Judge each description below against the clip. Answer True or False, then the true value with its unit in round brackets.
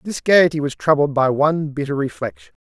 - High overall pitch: False (145 Hz)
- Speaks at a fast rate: False (180 wpm)